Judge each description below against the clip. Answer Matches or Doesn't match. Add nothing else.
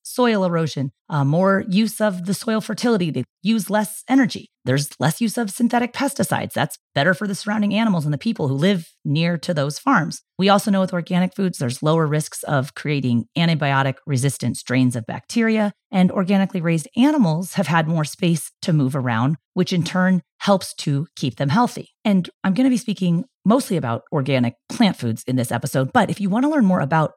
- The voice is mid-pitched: Matches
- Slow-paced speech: Doesn't match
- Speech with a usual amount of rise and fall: Doesn't match